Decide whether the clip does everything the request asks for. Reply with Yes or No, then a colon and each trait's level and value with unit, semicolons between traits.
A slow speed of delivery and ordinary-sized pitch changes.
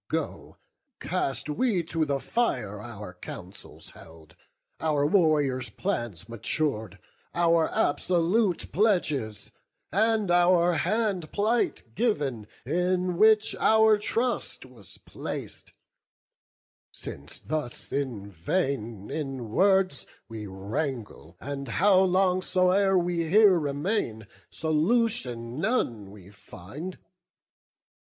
No: slow, 100 wpm; wide, 8.2 semitones